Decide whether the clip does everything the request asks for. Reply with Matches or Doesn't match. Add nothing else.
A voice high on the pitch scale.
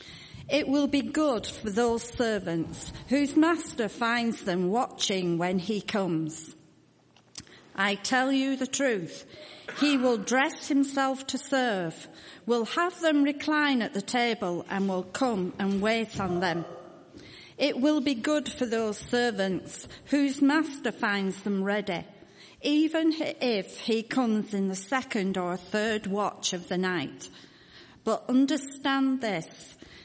Matches